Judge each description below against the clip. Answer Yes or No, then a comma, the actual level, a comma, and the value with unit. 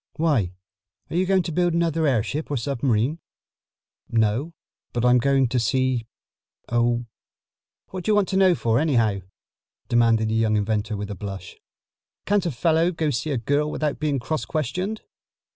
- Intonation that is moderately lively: No, wide, 6.1 semitones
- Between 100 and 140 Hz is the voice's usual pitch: Yes, low, 135 Hz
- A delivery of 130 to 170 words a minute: Yes, average, 165 wpm